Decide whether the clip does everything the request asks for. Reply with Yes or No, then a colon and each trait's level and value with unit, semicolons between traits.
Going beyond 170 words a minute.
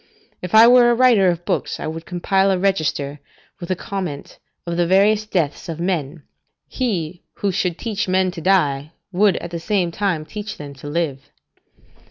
Yes: average, 185 wpm